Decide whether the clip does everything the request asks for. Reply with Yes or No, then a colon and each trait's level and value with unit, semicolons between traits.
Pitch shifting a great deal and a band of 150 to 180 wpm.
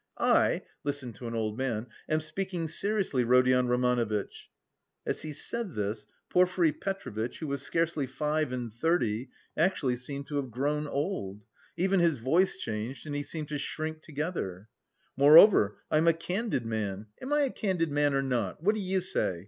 Yes: wide, 5.7 semitones; average, 170 wpm